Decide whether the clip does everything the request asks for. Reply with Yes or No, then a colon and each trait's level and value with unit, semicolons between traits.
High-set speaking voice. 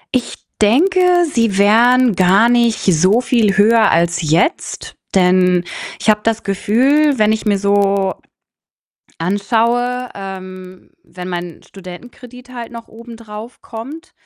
Yes: high, 215 Hz